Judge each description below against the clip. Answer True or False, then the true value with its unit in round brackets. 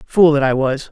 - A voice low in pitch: False (145 Hz)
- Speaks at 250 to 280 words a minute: True (265 wpm)